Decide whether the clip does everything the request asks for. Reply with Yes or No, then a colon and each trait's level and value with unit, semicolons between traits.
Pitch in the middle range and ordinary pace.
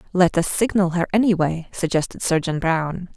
Yes: medium, 175 Hz; average, 150 wpm